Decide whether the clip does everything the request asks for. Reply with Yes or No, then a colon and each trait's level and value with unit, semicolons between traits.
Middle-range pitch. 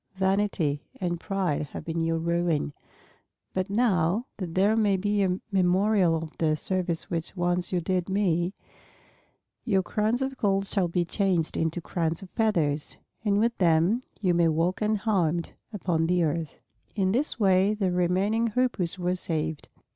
Yes: medium, 180 Hz